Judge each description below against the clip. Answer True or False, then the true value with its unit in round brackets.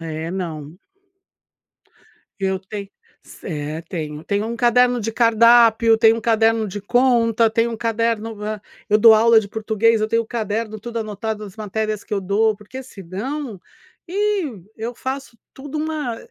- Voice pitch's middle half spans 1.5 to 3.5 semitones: True (2.4 semitones)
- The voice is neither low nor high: False (220 Hz)